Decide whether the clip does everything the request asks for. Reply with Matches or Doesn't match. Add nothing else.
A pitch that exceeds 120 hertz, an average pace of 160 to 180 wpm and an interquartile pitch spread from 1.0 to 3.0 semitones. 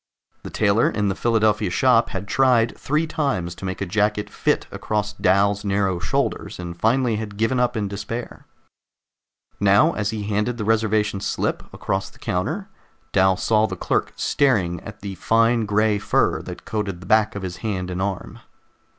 Doesn't match